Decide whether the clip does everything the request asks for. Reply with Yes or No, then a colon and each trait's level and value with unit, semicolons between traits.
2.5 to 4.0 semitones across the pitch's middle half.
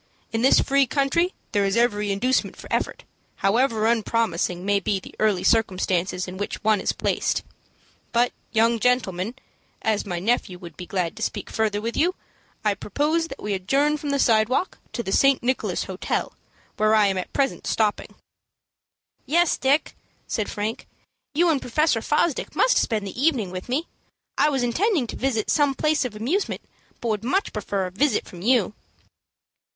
No: average, 5.3 semitones